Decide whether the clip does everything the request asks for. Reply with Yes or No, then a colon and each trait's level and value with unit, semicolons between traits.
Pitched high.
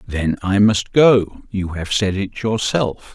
No: low, 100 Hz